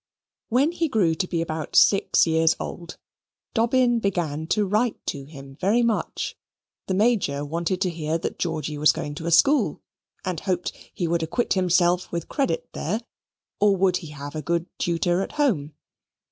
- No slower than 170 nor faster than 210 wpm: Yes, average, 175 wpm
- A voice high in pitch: No, medium, 175 Hz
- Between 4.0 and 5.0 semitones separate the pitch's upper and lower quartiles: Yes, average, 4.5 semitones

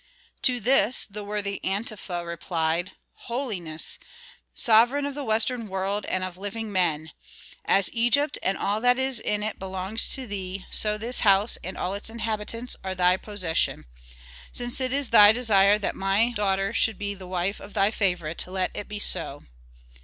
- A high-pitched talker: Yes, high, 205 Hz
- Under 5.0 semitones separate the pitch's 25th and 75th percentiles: Yes, average, 3.4 semitones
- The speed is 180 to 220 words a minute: No, average, 170 wpm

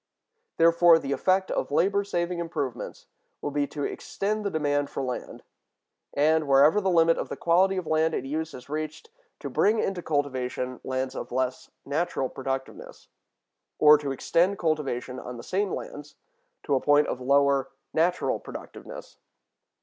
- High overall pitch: No, medium, 150 Hz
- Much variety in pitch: No, average, 4.2 semitones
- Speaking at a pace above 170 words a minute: No, average, 155 wpm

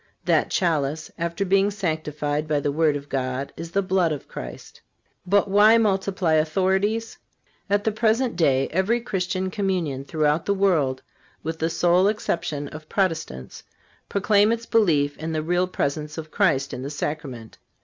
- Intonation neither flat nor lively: Yes, average, 4.9 semitones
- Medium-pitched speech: Yes, medium, 165 Hz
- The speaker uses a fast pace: No, average, 160 wpm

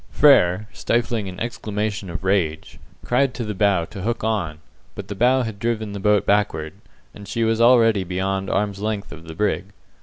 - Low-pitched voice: Yes, low, 105 Hz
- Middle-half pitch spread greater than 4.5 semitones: No, average, 2.9 semitones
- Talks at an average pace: Yes, average, 185 wpm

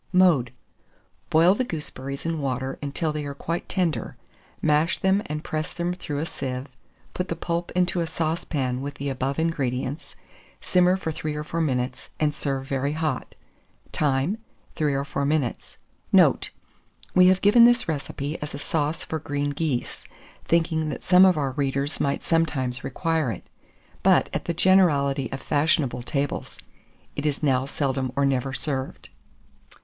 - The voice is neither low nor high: Yes, medium, 150 Hz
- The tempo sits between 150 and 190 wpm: Yes, average, 160 wpm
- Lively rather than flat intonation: No, average, 3.3 semitones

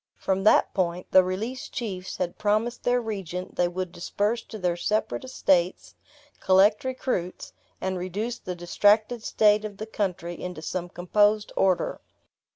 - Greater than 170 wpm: No, average, 150 wpm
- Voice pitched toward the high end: Yes, high, 195 Hz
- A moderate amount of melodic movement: Yes, average, 3.1 semitones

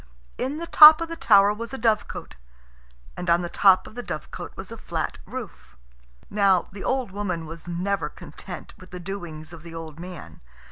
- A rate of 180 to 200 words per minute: Yes, average, 190 wpm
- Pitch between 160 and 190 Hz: Yes, medium, 185 Hz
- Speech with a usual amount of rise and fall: Yes, average, 4.2 semitones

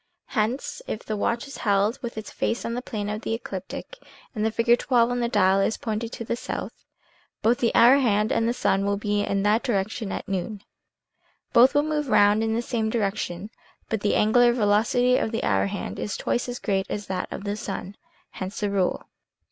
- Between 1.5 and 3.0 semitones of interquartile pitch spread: Yes, average, 2.7 semitones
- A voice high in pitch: Yes, high, 220 Hz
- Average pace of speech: No, fast, 210 wpm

